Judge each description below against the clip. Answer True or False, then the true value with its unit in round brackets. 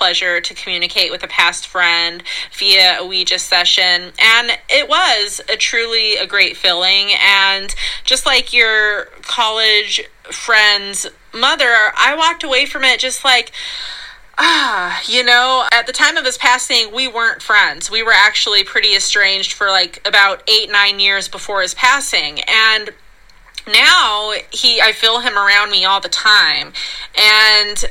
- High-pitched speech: True (215 Hz)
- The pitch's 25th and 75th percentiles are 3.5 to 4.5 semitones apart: True (4.1 semitones)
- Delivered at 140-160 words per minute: True (155 wpm)